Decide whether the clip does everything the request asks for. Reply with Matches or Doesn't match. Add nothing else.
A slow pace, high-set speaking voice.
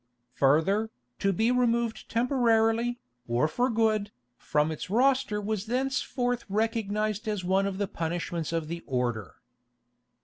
Matches